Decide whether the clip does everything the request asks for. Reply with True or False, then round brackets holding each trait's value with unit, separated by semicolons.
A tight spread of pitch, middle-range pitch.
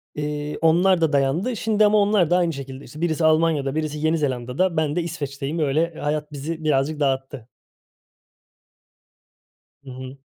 False (3.3 semitones; 155 Hz)